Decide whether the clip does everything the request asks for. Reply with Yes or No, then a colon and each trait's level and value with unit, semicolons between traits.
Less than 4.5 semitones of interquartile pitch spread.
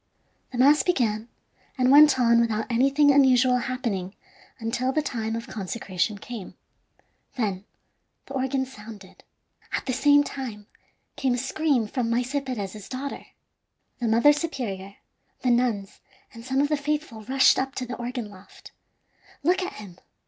Yes: average, 3.7 semitones